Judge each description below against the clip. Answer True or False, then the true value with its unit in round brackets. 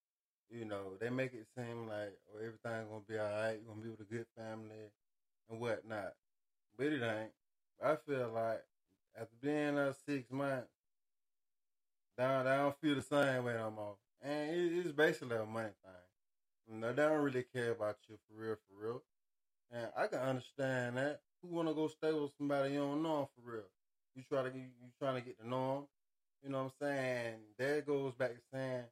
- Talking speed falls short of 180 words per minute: False (200 wpm)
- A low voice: True (125 Hz)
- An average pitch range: True (4.1 semitones)